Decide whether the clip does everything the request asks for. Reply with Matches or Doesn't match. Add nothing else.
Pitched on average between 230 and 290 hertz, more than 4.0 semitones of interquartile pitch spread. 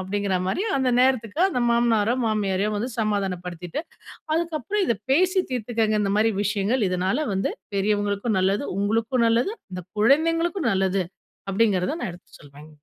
Doesn't match